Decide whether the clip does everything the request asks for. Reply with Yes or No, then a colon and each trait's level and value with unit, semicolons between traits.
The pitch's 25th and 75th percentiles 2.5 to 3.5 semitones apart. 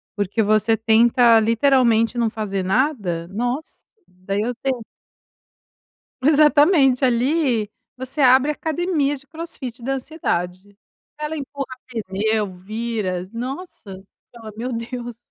No: average, 4.1 semitones